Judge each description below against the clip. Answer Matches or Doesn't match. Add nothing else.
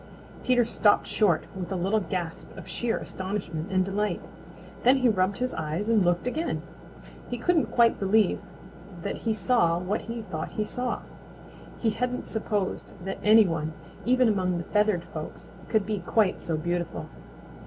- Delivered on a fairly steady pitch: Doesn't match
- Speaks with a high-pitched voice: Matches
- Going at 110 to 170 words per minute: Matches